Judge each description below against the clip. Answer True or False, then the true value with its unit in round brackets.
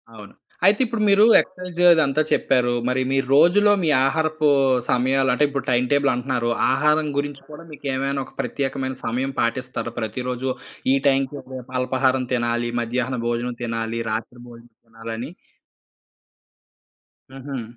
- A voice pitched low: True (130 Hz)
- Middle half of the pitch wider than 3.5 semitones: False (2.9 semitones)